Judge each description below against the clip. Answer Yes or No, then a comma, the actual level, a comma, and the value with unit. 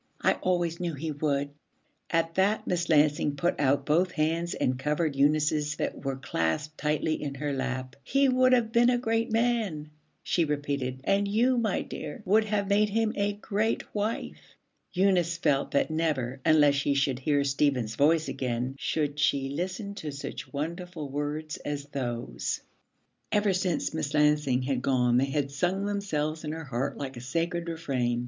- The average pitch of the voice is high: No, medium, 155 Hz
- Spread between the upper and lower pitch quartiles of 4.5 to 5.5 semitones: Yes, average, 4.8 semitones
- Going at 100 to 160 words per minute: No, average, 170 wpm